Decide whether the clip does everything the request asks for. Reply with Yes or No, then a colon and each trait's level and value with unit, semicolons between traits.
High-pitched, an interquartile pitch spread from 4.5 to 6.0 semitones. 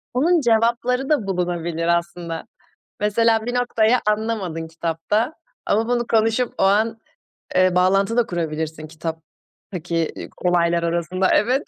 Yes: high, 195 Hz; average, 5.2 semitones